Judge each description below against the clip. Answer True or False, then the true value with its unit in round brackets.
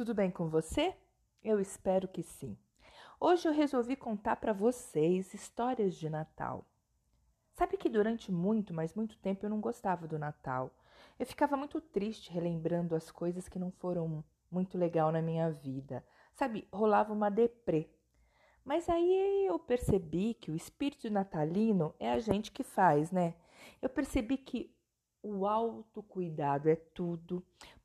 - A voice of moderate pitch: False (195 Hz)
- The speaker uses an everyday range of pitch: False (6.0 semitones)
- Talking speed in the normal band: True (150 wpm)